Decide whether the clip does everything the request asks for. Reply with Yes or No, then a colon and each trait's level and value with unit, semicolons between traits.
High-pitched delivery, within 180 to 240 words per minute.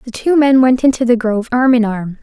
No: high, 240 Hz; fast, 270 wpm